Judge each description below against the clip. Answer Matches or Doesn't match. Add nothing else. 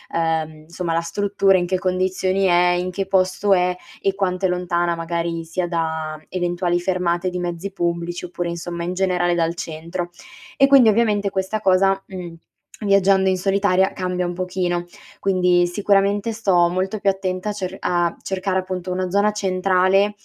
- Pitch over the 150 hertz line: Matches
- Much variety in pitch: Doesn't match